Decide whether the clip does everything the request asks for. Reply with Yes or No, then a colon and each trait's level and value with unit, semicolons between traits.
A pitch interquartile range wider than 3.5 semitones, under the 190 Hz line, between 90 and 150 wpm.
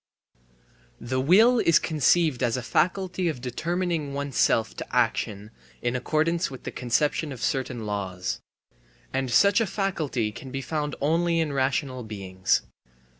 Yes: wide, 5.5 semitones; low, 135 Hz; average, 140 wpm